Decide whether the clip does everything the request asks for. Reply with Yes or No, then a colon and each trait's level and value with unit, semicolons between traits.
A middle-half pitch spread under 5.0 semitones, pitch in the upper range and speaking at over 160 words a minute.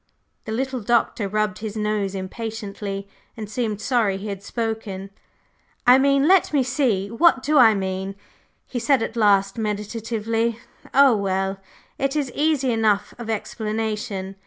No: average, 3.5 semitones; high, 220 Hz; average, 145 wpm